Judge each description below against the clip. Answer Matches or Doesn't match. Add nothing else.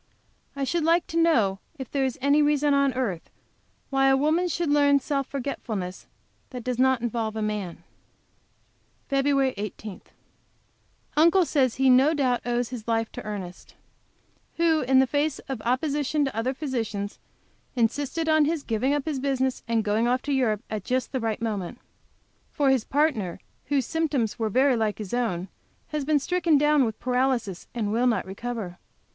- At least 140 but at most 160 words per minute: Doesn't match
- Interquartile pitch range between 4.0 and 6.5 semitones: Matches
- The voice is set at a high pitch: Matches